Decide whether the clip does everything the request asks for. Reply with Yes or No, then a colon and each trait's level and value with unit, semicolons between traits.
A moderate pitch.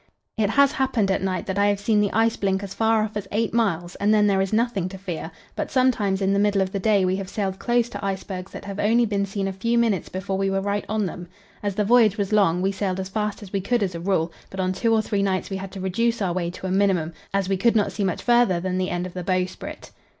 No: high, 195 Hz